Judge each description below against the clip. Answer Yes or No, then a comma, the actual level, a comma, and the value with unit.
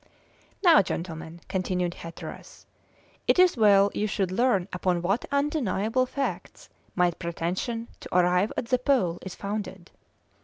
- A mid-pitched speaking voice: No, high, 195 Hz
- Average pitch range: Yes, average, 5.0 semitones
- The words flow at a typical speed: No, slow, 130 wpm